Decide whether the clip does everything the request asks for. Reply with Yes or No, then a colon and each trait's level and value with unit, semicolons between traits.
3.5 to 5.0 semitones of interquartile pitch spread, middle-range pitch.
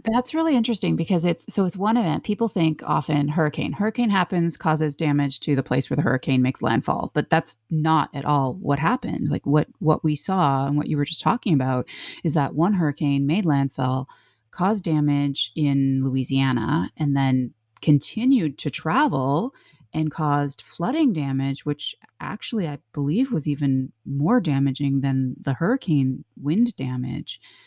Yes: average, 4.1 semitones; medium, 150 Hz